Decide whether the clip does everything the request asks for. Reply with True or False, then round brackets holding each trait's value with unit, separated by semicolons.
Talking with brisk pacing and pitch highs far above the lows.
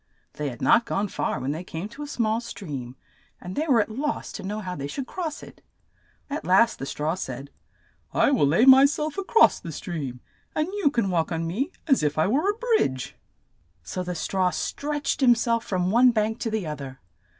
True (215 wpm; 9.0 semitones)